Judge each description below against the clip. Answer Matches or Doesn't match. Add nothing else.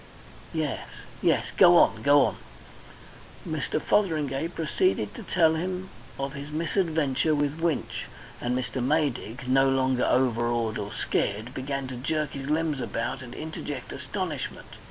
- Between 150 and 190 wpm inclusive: Doesn't match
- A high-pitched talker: Doesn't match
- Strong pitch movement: Doesn't match